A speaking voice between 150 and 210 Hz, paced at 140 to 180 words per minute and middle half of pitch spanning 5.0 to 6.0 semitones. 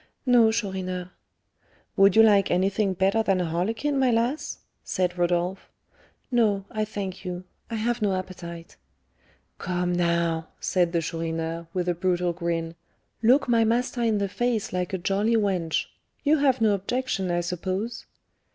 No: high, 190 Hz; average, 150 wpm; average, 4.1 semitones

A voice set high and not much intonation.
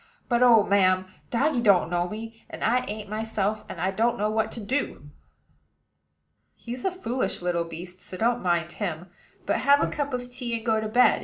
No: high, 220 Hz; average, 4.6 semitones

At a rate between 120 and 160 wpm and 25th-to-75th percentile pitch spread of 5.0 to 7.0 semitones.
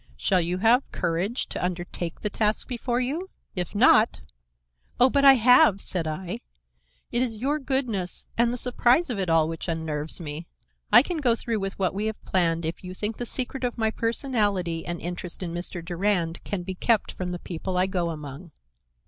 No: average, 190 wpm; wide, 5.6 semitones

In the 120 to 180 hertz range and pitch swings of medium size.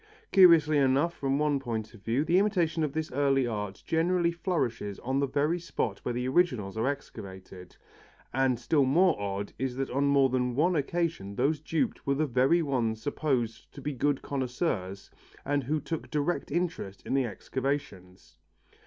Yes: low, 135 Hz; average, 4.8 semitones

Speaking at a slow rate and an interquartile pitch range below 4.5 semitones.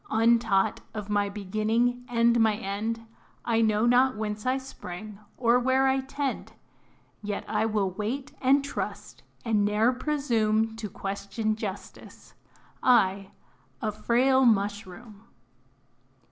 Yes: slow, 120 wpm; average, 2.9 semitones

